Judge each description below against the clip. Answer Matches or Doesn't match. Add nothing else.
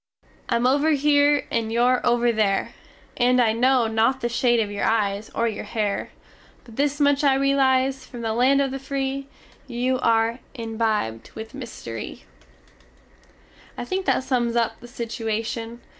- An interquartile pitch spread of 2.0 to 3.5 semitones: Matches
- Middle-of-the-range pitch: Doesn't match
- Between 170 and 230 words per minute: Doesn't match